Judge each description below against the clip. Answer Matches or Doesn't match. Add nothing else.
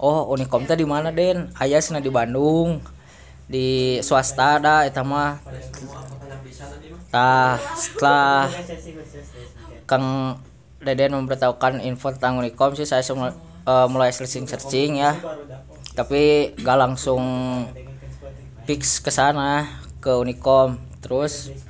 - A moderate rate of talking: Matches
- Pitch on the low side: Matches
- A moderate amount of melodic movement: Doesn't match